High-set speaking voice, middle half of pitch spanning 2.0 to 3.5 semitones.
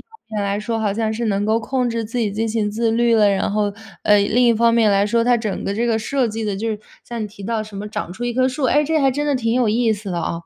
Yes: high, 225 Hz; narrow, 2.4 semitones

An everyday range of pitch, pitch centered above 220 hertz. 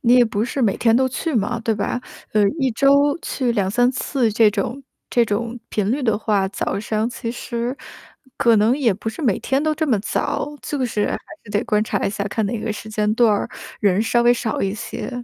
Yes: average, 3.0 semitones; high, 230 Hz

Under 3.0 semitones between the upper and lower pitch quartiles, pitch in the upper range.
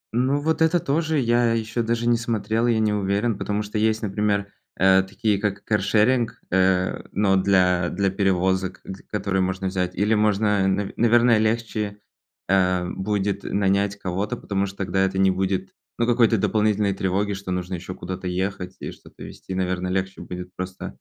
No: narrow, 2.5 semitones; low, 100 Hz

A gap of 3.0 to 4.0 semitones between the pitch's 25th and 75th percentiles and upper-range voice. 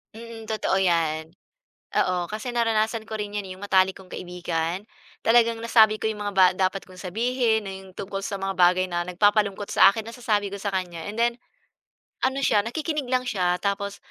Yes: average, 3.3 semitones; high, 205 Hz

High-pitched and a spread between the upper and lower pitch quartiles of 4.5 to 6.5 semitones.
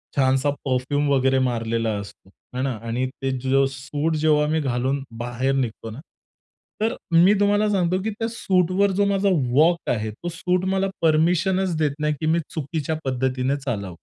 No: medium, 145 Hz; average, 5.3 semitones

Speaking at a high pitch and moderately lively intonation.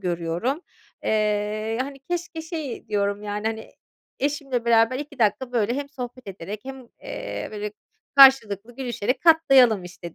Yes: high, 235 Hz; average, 4.7 semitones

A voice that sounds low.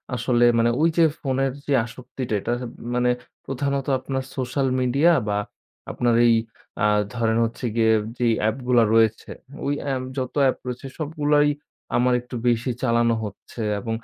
Yes: low, 125 Hz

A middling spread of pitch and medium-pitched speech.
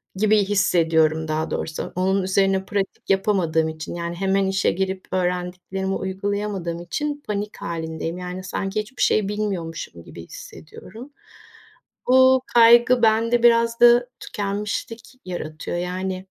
No: average, 3.4 semitones; high, 195 Hz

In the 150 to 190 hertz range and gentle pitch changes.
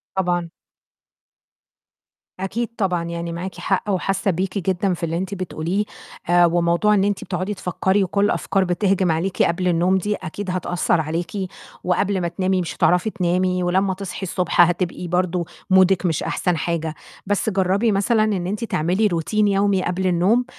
Yes: medium, 185 Hz; narrow, 2.0 semitones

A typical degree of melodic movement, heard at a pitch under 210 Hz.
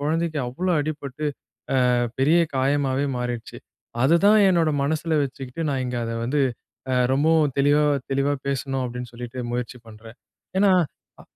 Yes: average, 3.7 semitones; medium, 140 Hz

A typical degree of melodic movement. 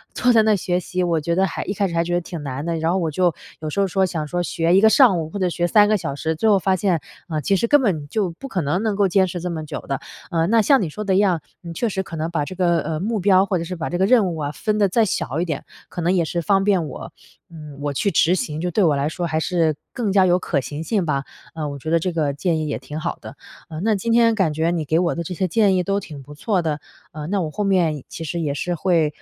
Yes: average, 3.7 semitones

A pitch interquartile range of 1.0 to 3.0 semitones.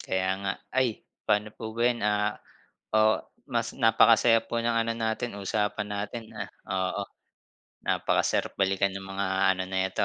Yes: average, 2.7 semitones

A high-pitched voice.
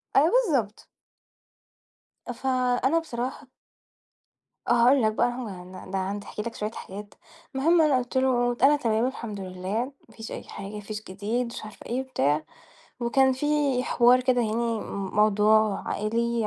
Yes: high, 235 Hz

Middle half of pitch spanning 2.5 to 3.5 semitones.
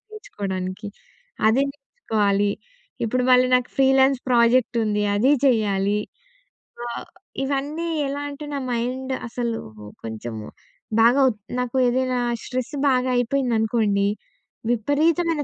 No: average, 4.0 semitones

